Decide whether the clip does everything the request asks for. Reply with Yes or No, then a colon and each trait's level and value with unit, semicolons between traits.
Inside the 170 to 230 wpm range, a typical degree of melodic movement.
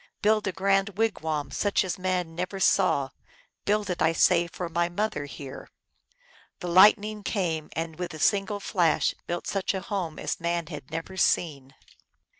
Yes: average, 180 wpm; average, 3.5 semitones